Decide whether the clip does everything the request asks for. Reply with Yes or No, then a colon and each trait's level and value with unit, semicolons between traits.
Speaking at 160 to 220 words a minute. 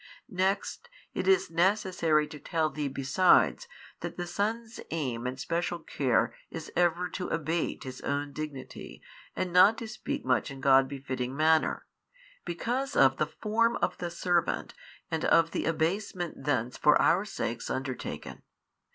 No: average, 150 wpm